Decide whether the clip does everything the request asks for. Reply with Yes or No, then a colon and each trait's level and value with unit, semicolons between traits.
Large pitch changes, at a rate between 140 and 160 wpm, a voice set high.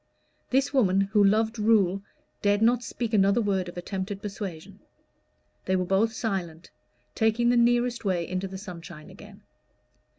No: average, 3.0 semitones; average, 145 wpm; high, 200 Hz